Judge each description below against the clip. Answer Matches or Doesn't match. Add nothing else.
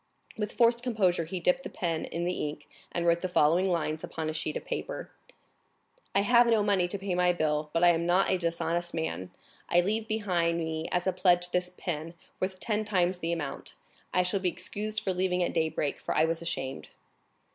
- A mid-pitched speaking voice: Matches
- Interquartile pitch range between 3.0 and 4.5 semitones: Doesn't match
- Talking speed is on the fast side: Matches